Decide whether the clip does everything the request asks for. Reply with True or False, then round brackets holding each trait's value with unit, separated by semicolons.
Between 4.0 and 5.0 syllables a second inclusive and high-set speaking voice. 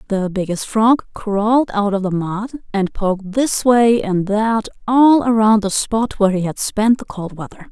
True (4.4 syllables/s; 210 Hz)